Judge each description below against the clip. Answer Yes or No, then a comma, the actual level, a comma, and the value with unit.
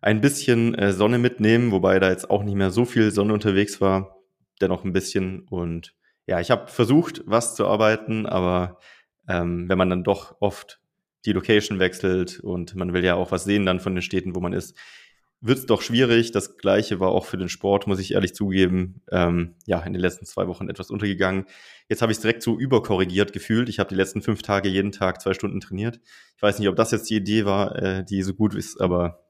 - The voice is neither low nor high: No, low, 100 Hz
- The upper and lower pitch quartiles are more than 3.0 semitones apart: No, narrow, 2.4 semitones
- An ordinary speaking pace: No, fast, 220 wpm